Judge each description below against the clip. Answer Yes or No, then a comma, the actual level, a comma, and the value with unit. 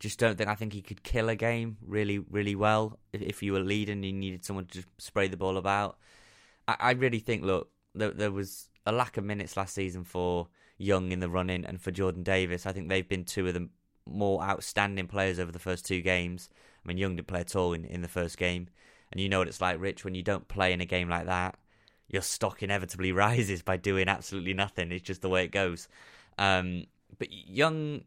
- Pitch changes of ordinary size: No, narrow, 1.8 semitones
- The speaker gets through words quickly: Yes, fast, 235 wpm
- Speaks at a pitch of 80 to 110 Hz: Yes, very low, 95 Hz